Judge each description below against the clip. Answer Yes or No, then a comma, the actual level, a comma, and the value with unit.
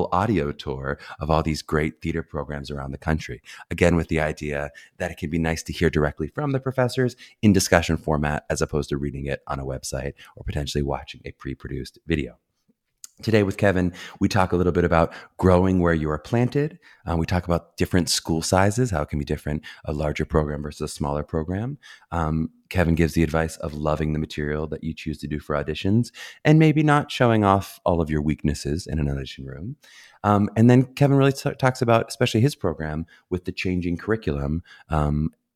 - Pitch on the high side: No, very low, 80 Hz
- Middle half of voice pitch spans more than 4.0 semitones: Yes, average, 4.7 semitones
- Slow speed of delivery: No, fast, 205 wpm